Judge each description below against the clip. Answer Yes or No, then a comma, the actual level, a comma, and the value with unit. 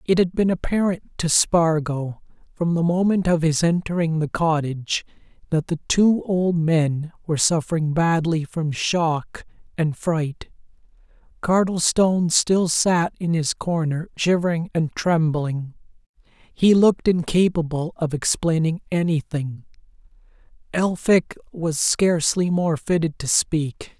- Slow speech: Yes, slow, 120 wpm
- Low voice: No, medium, 165 Hz